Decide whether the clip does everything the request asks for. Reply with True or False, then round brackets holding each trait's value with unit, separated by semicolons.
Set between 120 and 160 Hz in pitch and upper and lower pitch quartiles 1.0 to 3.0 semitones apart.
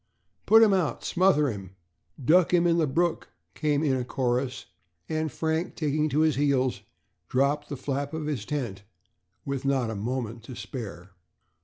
False (140 Hz; 4.0 semitones)